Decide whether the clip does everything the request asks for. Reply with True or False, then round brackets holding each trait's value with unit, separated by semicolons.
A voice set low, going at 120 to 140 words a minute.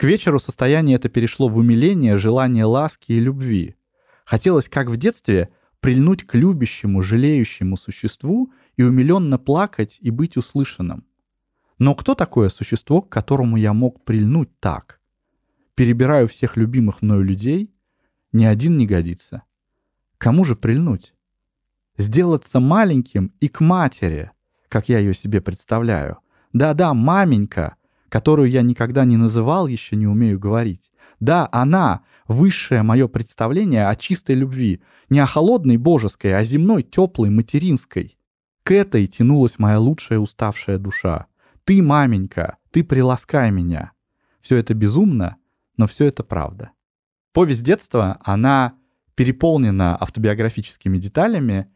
True (120 Hz; 130 wpm)